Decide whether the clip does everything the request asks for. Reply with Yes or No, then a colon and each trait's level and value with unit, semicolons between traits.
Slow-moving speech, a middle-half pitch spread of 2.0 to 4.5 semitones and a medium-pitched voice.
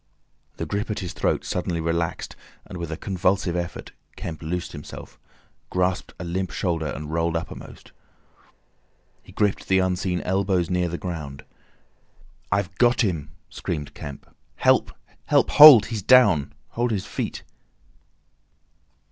No: slow, 130 wpm; average, 2.8 semitones; very low, 90 Hz